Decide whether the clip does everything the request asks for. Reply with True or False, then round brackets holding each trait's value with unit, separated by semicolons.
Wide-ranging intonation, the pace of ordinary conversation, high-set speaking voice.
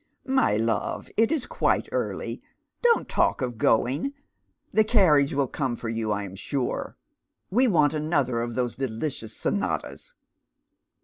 False (7.8 semitones; 150 wpm; 135 Hz)